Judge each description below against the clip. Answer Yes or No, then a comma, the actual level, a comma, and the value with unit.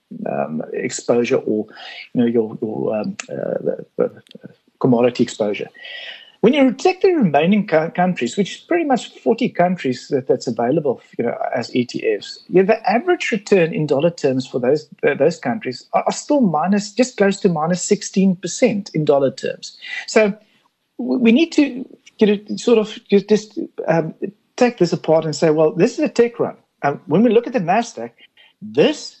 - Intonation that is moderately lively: No, wide, 6.7 semitones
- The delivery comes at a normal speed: Yes, average, 180 wpm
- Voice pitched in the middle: No, high, 210 Hz